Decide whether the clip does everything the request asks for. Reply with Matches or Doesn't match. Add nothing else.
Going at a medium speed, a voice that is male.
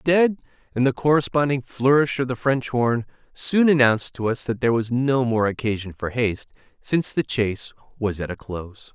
Matches